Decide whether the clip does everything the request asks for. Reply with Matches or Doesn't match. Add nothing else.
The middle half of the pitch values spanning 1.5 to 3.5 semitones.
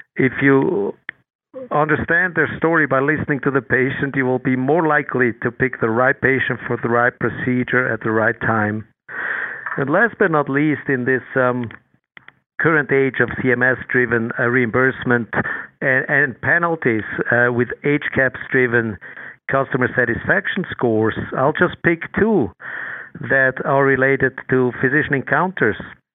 Matches